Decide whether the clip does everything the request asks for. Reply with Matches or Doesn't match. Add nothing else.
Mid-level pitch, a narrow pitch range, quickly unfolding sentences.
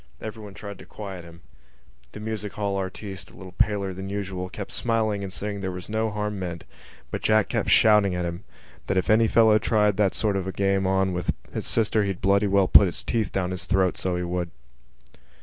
Doesn't match